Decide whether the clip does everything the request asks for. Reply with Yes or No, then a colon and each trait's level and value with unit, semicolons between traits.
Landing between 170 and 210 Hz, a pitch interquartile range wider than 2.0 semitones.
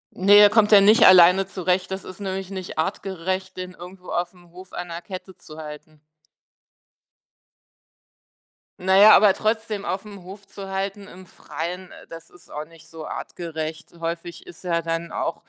Yes: medium, 185 Hz; narrow, 2.4 semitones